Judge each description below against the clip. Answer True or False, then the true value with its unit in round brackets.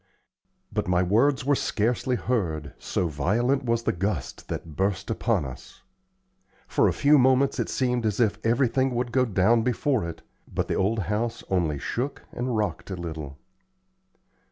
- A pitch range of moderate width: False (5.7 semitones)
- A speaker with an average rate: True (160 wpm)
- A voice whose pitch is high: False (115 Hz)